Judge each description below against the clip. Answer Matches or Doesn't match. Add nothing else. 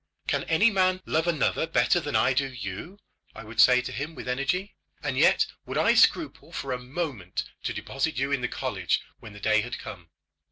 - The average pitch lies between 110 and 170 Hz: Matches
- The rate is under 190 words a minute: Doesn't match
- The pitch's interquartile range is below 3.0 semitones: Doesn't match